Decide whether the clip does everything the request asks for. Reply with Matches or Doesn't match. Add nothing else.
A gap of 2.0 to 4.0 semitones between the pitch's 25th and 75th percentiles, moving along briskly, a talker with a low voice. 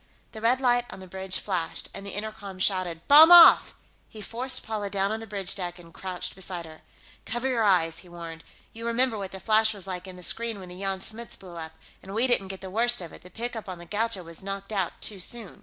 Doesn't match